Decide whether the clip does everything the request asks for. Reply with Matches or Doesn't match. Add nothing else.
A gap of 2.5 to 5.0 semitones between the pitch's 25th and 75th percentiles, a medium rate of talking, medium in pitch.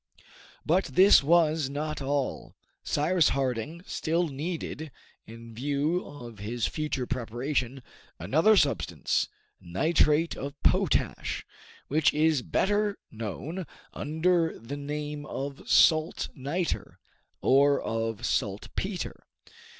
Doesn't match